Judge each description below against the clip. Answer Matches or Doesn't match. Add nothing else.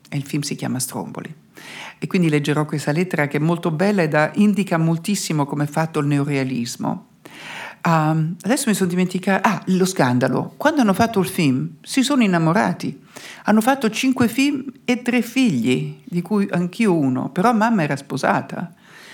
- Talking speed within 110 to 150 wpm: Doesn't match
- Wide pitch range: Matches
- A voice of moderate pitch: Matches